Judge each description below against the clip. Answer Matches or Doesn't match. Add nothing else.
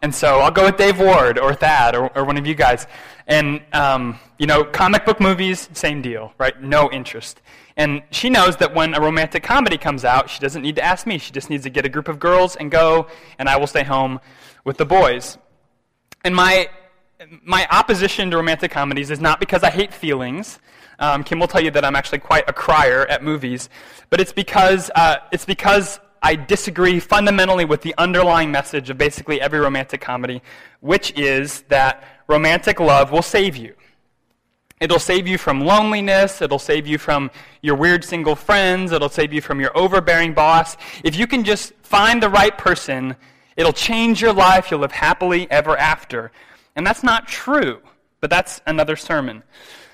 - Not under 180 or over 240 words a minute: Matches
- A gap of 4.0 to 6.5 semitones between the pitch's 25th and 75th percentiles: Matches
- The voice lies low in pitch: Doesn't match